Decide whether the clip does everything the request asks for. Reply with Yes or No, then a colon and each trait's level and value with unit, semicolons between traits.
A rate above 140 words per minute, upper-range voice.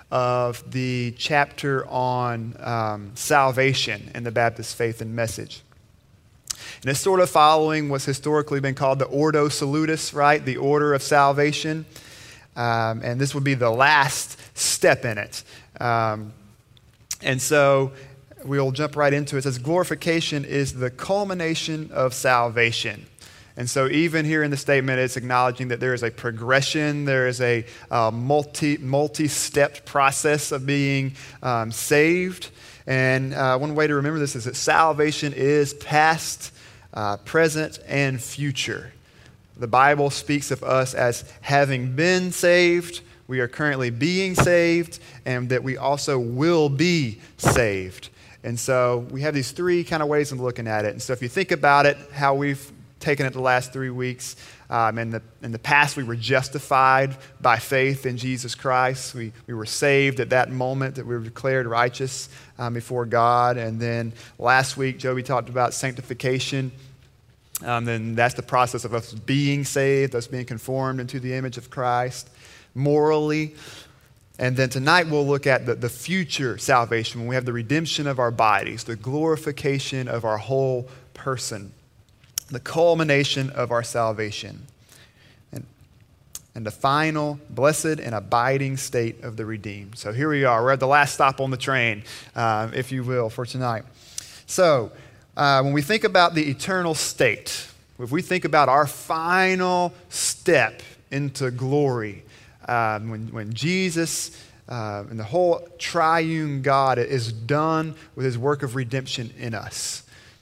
No: average, 160 wpm; low, 130 Hz